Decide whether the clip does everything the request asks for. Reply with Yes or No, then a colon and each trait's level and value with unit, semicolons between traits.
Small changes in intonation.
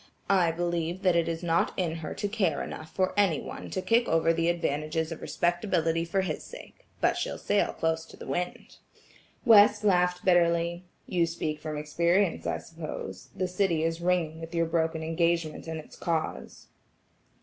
Yes: narrow, 1.7 semitones